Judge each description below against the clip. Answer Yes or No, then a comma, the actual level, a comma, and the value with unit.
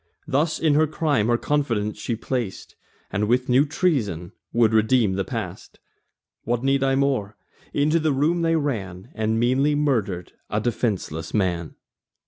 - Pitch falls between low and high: No, low, 120 Hz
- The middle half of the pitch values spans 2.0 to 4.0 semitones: No, wide, 5.5 semitones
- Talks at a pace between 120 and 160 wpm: Yes, average, 150 wpm